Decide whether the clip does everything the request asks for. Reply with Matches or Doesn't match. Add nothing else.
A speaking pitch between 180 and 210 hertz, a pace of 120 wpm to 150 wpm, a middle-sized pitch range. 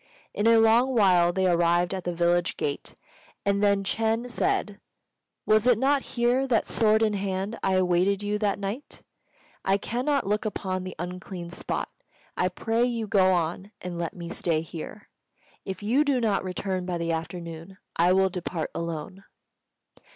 Doesn't match